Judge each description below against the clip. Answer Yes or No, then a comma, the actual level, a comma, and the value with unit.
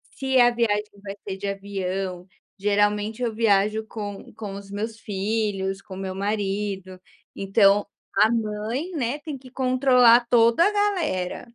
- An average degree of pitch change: Yes, average, 3.2 semitones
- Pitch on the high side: Yes, high, 210 Hz